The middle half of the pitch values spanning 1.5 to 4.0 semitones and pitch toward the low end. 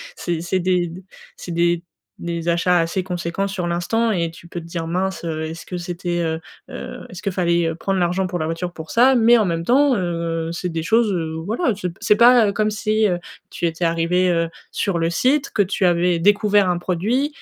No: average, 3.3 semitones; medium, 175 Hz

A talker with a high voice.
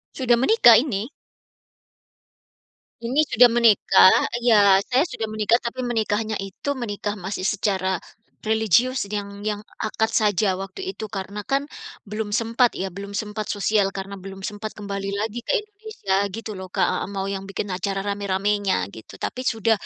Yes: high, 210 Hz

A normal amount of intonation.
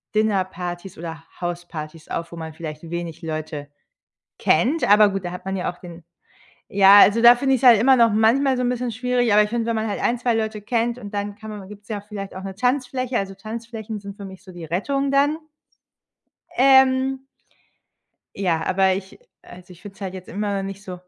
Yes: average, 4.6 semitones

